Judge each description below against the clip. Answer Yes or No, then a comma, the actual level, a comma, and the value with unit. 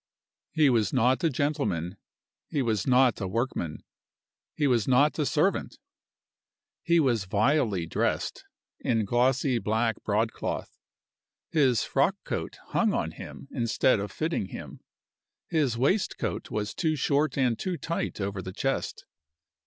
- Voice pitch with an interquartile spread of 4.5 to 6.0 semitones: Yes, average, 5.2 semitones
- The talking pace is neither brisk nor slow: No, slow, 130 wpm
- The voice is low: Yes, low, 125 Hz